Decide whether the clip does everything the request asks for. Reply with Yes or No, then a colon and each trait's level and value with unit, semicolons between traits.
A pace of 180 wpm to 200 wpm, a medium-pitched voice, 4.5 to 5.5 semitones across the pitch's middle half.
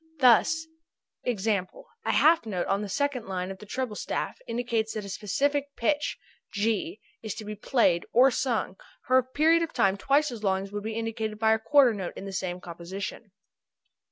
No: average, 190 wpm; high, 220 Hz; average, 4.9 semitones